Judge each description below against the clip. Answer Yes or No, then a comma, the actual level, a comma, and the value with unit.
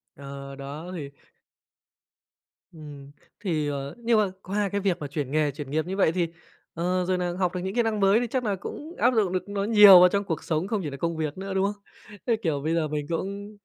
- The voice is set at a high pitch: No, medium, 180 Hz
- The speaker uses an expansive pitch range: No, average, 4.8 semitones